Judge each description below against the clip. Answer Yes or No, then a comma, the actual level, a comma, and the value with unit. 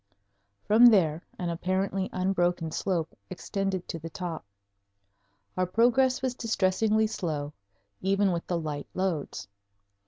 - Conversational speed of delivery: No, slow, 120 wpm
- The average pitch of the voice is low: No, medium, 185 Hz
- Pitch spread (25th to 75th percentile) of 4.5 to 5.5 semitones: No, average, 3.4 semitones